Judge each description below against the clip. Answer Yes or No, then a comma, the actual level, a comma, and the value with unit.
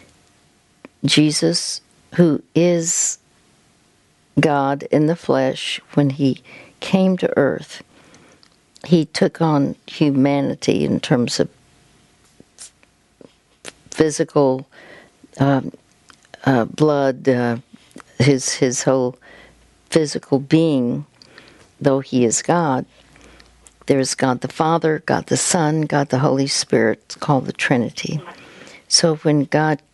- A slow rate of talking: Yes, slow, 100 wpm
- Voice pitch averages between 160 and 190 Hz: No, medium, 145 Hz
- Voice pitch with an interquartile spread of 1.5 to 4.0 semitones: Yes, average, 3.3 semitones